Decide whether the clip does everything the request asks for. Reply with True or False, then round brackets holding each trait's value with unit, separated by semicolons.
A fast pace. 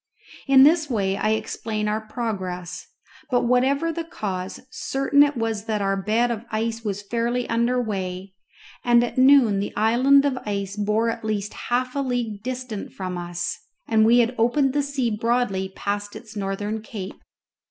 False (170 wpm)